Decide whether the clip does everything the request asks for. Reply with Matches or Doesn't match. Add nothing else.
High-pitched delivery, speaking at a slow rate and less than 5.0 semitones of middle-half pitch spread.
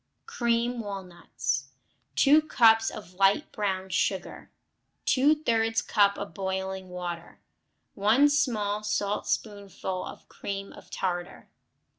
Matches